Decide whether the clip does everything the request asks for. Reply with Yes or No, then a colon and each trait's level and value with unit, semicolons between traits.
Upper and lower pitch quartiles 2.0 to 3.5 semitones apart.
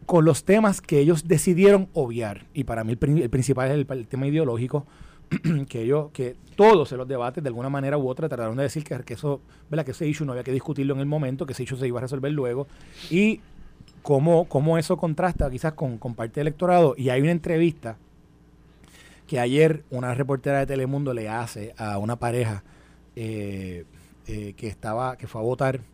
No: average, 4.3 semitones